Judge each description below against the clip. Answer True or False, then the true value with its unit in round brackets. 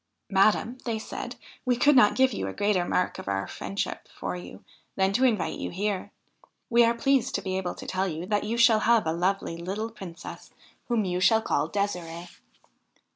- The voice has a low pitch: False (200 Hz)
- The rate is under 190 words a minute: False (205 wpm)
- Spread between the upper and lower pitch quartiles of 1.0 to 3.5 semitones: False (4.2 semitones)